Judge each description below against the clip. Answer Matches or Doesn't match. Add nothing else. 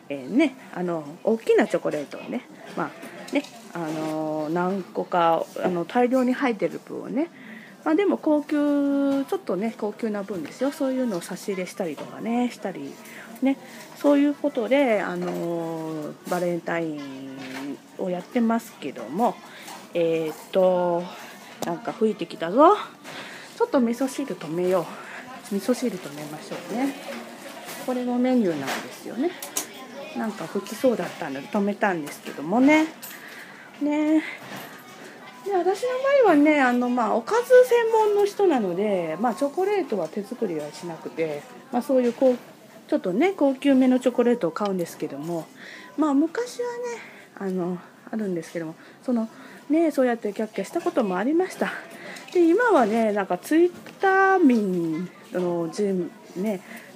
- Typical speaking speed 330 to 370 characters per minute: Doesn't match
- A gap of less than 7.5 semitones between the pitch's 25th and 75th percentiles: Doesn't match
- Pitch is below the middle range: Doesn't match